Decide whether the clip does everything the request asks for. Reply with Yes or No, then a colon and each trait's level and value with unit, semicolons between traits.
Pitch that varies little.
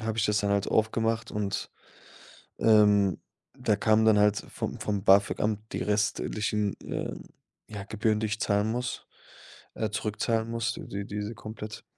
Yes: narrow, 1.4 semitones